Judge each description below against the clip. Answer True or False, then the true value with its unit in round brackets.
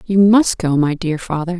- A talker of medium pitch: True (175 Hz)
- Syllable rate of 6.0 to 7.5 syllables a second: False (4.8 syllables/s)